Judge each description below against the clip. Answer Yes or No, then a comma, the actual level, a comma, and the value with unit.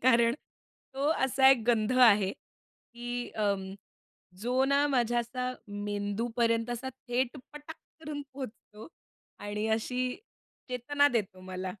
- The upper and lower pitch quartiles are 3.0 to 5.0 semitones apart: Yes, average, 3.6 semitones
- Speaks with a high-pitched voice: Yes, high, 240 Hz